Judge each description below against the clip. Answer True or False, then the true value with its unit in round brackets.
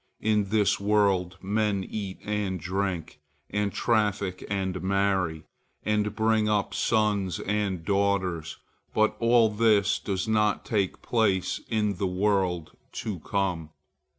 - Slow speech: True (125 wpm)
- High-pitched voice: False (100 Hz)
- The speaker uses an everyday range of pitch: False (2.2 semitones)